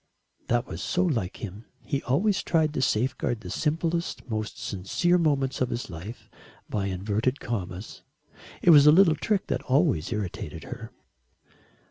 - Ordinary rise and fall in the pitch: No, wide, 7.0 semitones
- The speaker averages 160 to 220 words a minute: No, average, 150 wpm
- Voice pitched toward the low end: Yes, low, 130 Hz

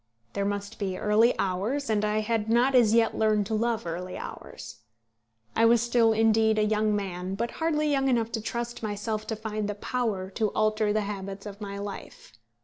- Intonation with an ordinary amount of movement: No, narrow, 2.1 semitones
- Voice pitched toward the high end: Yes, high, 215 Hz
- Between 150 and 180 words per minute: No, average, 195 wpm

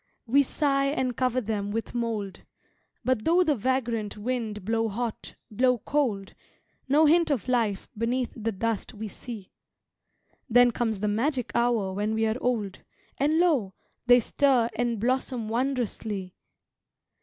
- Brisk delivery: No, average, 145 wpm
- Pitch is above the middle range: Yes, high, 235 Hz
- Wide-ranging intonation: No, average, 3.2 semitones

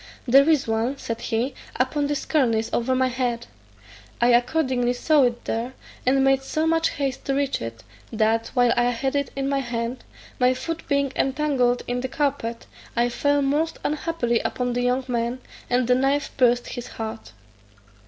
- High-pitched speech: Yes, very high, 255 Hz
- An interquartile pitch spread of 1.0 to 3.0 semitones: Yes, narrow, 2.6 semitones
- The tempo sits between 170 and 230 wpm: Yes, average, 175 wpm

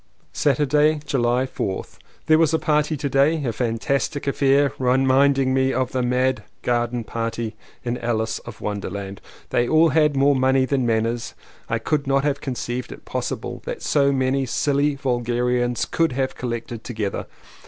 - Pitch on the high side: No, low, 130 Hz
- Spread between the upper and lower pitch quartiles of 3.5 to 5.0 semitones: No, average, 2.7 semitones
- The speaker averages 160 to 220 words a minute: Yes, average, 165 wpm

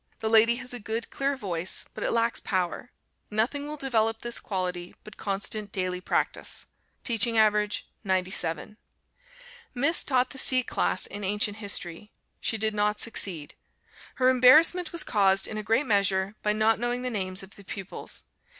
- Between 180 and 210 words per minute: No, average, 165 wpm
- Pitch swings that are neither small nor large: Yes, average, 3.9 semitones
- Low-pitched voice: No, high, 215 Hz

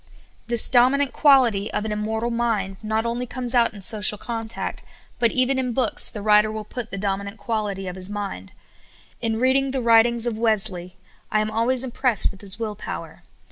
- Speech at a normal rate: Yes, average, 185 wpm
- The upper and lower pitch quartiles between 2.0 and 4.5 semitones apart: Yes, narrow, 2.6 semitones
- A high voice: Yes, high, 225 Hz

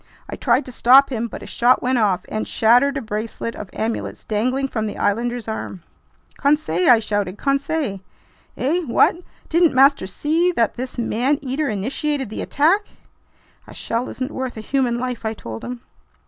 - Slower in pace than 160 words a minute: No, average, 175 wpm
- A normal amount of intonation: Yes, average, 4.0 semitones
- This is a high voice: Yes, high, 245 Hz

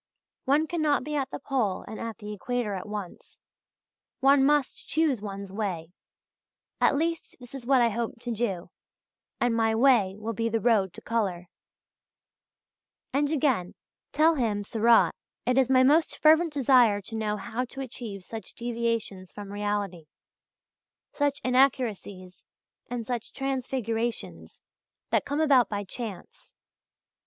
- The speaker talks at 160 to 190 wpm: No, average, 145 wpm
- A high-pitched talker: Yes, high, 235 Hz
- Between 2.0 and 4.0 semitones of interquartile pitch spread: No, average, 4.6 semitones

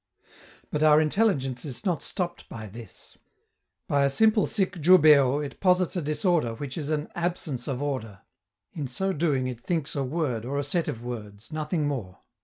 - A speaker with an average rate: Yes, average, 180 wpm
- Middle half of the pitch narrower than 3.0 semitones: No, average, 5.1 semitones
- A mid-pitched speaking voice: Yes, medium, 145 Hz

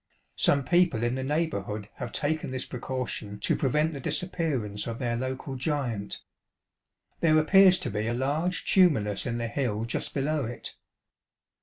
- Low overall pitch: Yes, low, 130 Hz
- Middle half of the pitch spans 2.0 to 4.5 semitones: No, average, 5.0 semitones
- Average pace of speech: Yes, average, 155 wpm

